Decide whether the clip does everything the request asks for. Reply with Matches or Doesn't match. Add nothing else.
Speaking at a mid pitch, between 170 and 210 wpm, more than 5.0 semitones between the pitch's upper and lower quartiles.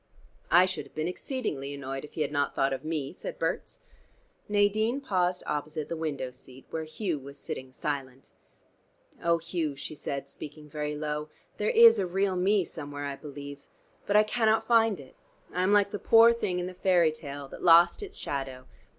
Matches